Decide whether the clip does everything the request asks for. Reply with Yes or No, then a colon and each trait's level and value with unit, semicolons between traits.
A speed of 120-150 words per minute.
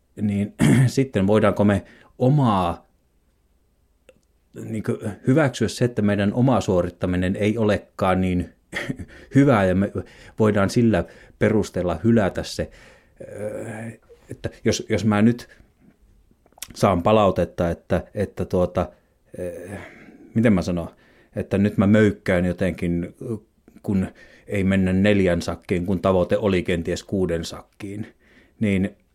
No: average, 110 wpm